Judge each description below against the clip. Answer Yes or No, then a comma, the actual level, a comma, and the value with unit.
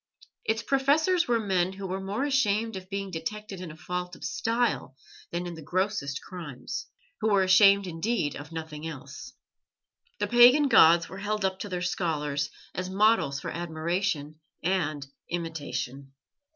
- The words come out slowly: No, average, 155 wpm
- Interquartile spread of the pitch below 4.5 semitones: No, average, 4.8 semitones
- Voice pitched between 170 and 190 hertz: Yes, medium, 185 Hz